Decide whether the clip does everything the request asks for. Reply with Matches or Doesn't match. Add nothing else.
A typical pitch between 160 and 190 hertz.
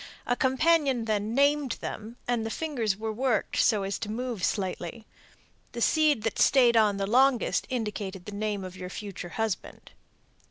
Doesn't match